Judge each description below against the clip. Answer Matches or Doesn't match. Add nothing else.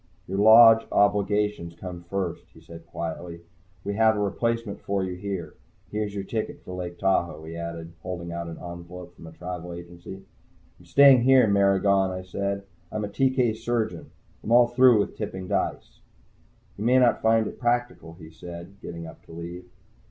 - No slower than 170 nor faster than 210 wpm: Matches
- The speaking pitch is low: Matches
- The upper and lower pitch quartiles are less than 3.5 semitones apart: Doesn't match